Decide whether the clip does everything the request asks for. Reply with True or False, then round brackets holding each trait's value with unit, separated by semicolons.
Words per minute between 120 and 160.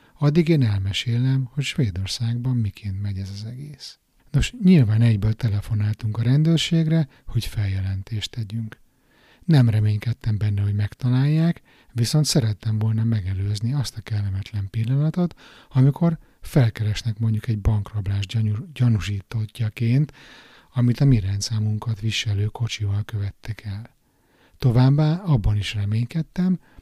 False (110 wpm)